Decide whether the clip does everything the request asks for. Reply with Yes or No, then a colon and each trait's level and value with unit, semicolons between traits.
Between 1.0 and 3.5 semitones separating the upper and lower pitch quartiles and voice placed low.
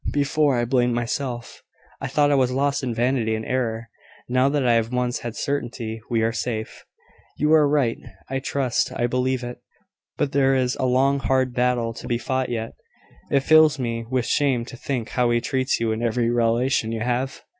Yes: narrow, 2.4 semitones; low, 125 Hz